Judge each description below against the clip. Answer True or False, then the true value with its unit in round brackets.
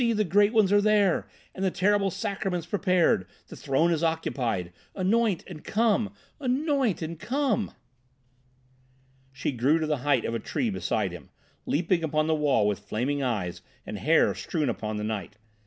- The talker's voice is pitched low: False (165 Hz)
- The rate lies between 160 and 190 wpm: True (165 wpm)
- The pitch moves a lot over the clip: True (8.2 semitones)